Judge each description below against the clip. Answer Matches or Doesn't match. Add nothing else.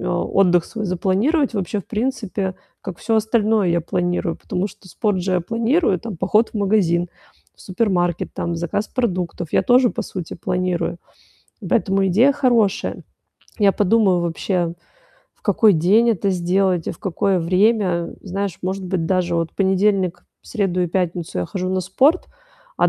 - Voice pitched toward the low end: Doesn't match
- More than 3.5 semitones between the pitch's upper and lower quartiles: Doesn't match